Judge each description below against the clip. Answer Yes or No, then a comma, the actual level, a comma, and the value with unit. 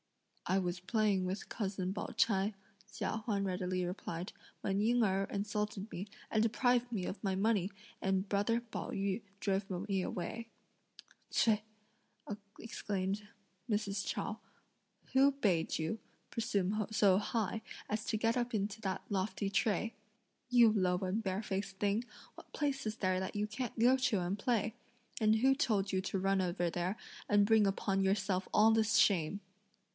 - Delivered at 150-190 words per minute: Yes, average, 155 wpm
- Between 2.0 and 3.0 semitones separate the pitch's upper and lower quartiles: Yes, narrow, 2.6 semitones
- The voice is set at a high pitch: Yes, high, 205 Hz